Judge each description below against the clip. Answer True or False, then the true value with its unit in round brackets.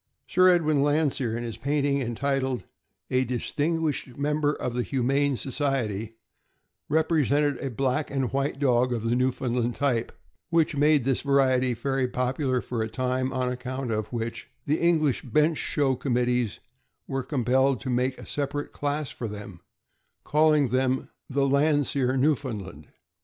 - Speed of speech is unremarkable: True (150 wpm)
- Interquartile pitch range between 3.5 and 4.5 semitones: False (2.7 semitones)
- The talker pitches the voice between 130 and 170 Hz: True (135 Hz)